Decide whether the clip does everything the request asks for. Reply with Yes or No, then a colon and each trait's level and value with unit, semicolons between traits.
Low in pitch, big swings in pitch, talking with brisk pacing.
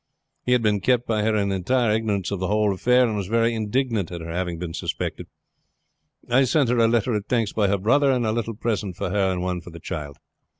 No: low, 105 Hz; average, 3.9 semitones; fast, 245 wpm